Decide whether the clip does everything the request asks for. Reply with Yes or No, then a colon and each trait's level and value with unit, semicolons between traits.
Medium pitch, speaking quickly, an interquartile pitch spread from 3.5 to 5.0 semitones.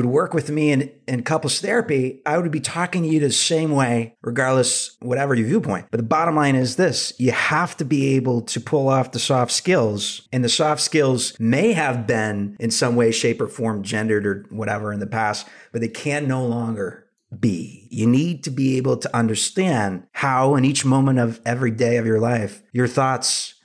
No: low, 130 Hz; fast, 210 wpm; average, 4.0 semitones